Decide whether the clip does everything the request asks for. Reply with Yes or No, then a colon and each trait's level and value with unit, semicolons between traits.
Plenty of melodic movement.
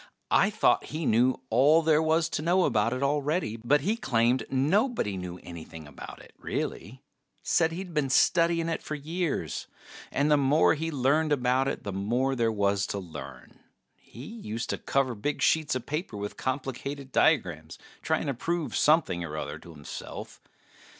Yes: wide, 6.2 semitones